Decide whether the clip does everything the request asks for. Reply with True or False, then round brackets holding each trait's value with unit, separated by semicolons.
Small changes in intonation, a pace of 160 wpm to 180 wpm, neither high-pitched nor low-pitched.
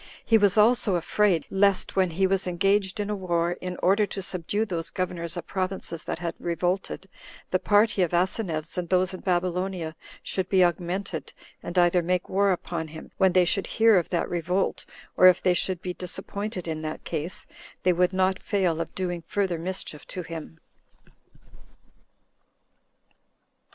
True (2.0 semitones; 165 wpm; 180 Hz)